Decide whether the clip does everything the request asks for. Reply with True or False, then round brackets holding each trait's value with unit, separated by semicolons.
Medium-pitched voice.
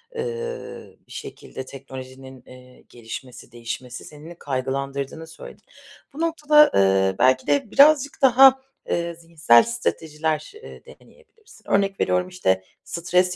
True (160 Hz)